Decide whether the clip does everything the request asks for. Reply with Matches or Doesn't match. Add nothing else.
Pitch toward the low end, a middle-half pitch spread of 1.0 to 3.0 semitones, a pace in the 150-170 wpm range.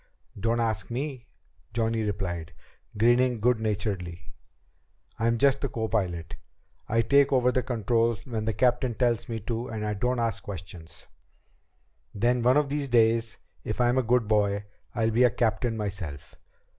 Matches